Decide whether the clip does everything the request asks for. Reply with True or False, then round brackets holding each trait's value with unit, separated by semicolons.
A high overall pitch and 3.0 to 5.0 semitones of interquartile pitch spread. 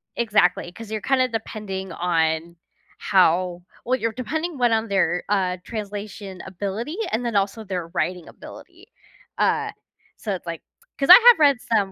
True (205 Hz; 4.6 semitones)